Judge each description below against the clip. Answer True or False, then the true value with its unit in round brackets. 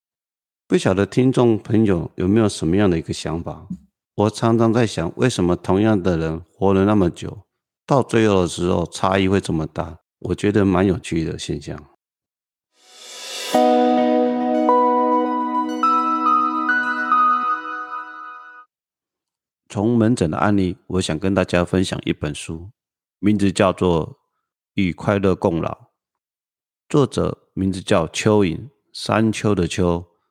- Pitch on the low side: True (95 Hz)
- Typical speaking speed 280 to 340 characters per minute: False (180 characters per minute)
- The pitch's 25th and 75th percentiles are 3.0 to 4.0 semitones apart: False (4.8 semitones)